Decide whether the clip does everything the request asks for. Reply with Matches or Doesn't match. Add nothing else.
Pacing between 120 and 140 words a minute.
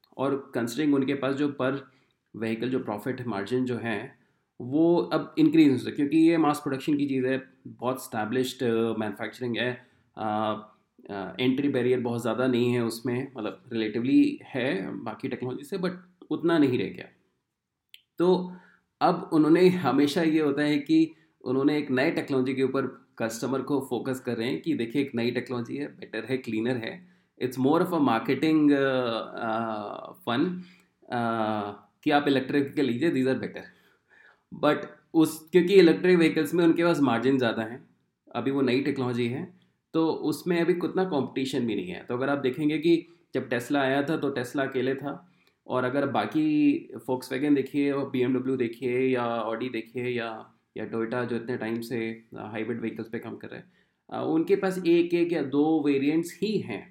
Doesn't match